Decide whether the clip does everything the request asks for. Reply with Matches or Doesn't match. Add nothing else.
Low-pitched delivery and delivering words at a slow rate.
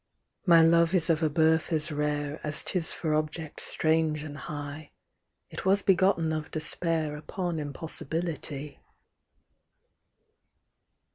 Doesn't match